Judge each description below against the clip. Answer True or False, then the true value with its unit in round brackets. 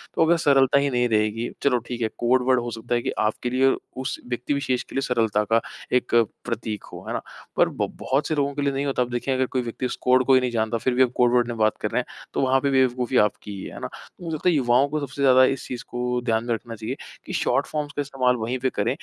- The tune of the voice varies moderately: False (2.2 semitones)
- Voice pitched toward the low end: True (125 Hz)